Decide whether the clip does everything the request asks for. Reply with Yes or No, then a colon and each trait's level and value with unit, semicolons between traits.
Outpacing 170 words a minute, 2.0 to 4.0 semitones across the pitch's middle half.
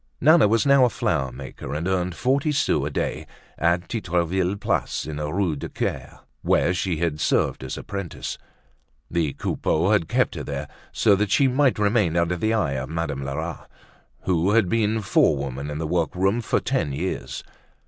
No: average, 180 wpm; wide, 5.6 semitones